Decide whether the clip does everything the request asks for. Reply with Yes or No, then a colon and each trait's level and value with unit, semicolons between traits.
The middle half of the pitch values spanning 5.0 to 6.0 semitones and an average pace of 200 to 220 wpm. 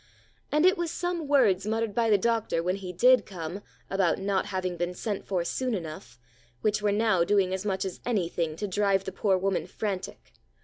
No: average, 3.3 semitones; fast, 205 wpm